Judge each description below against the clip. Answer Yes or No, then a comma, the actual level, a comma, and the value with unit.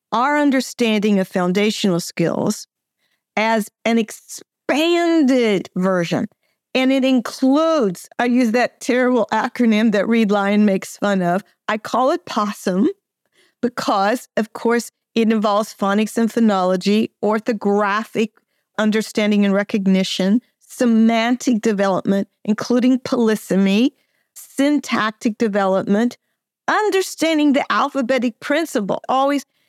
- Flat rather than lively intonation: No, average, 3.9 semitones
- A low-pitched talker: No, high, 225 Hz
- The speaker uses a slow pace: Yes, slow, 100 wpm